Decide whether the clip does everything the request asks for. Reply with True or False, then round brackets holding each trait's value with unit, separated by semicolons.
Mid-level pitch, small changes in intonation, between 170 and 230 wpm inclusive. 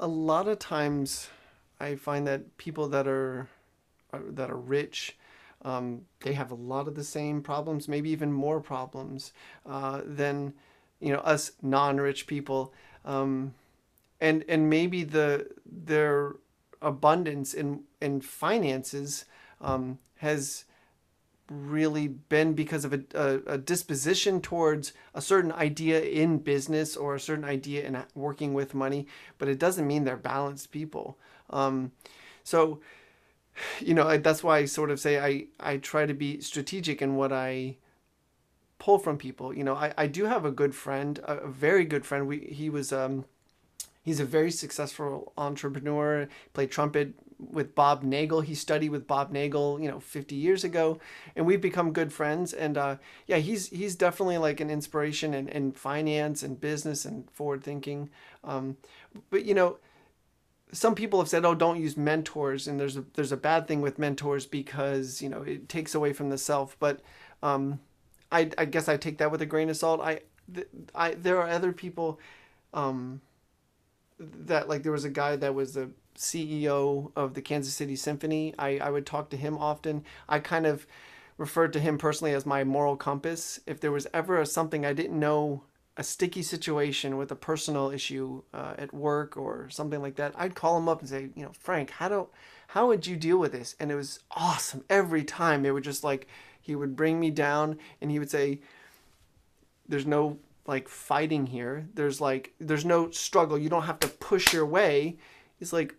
True (145 Hz; 2.0 semitones; 180 wpm)